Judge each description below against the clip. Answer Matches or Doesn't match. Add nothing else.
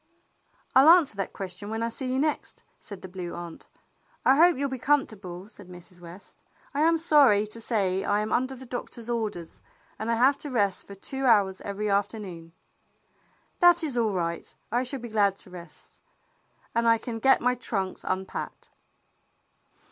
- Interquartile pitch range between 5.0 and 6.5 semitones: Matches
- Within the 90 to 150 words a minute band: Doesn't match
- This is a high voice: Matches